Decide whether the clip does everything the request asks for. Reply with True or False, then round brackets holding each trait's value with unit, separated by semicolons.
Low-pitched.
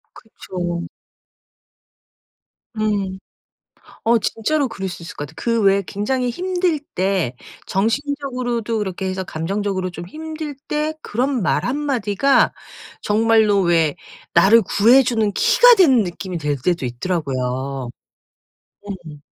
False (210 Hz)